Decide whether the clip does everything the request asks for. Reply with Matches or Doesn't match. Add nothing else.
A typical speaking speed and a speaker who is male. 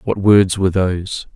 Matches